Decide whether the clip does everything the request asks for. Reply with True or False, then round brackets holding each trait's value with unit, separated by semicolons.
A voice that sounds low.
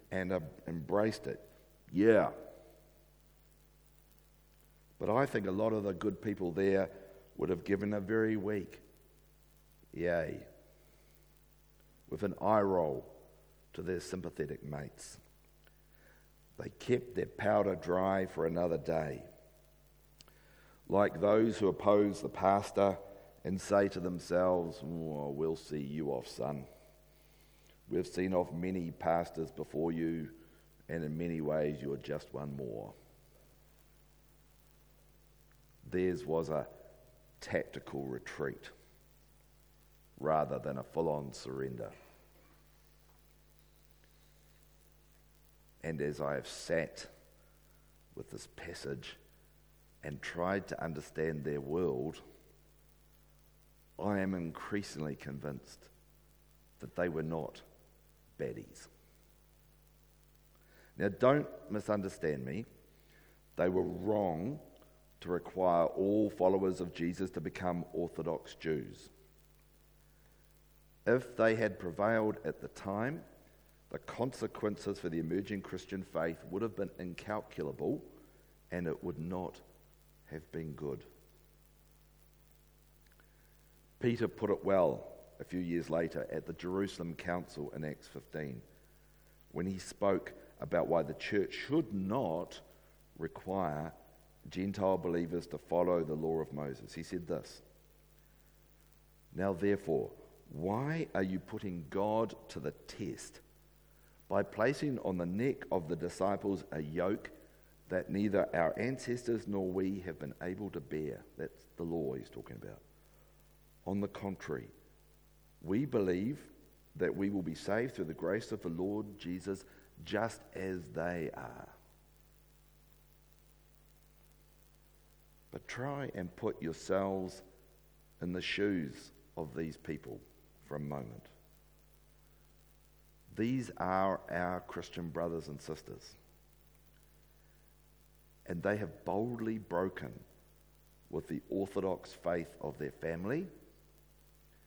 True (90 Hz)